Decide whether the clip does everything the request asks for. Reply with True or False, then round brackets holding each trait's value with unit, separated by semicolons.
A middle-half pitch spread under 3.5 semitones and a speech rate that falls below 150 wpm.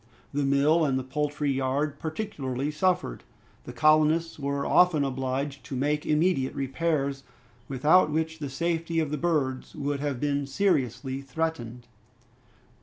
True (2.9 semitones; 135 wpm)